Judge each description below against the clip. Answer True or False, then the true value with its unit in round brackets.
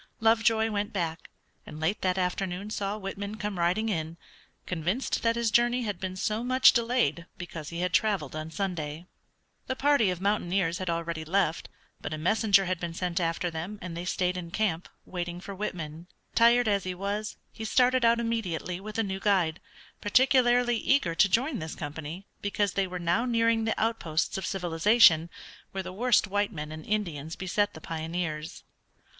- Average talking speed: True (180 wpm)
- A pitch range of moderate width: True (4.5 semitones)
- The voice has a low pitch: False (190 Hz)